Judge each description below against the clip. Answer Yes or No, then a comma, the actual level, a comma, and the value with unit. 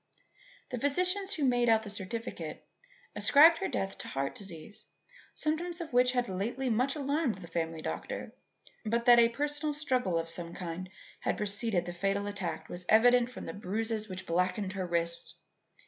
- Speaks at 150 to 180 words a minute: Yes, average, 170 wpm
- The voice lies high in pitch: Yes, high, 220 Hz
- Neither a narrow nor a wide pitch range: No, wide, 5.8 semitones